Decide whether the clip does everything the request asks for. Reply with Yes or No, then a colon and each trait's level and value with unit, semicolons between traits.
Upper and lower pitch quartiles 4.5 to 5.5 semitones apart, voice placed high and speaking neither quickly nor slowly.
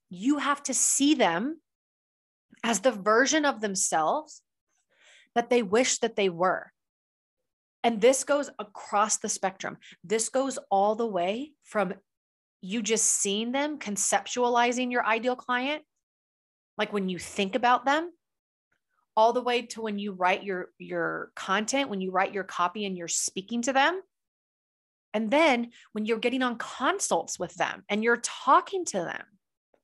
Yes: average, 4.8 semitones; high, 235 Hz; average, 155 wpm